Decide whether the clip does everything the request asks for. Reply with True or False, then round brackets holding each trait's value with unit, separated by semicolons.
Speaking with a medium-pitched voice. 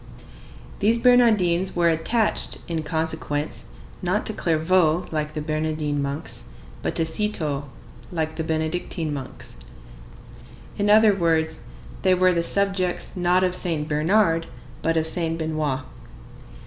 True (165 Hz)